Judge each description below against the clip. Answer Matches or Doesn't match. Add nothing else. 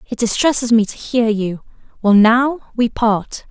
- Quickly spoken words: Doesn't match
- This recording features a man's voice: Doesn't match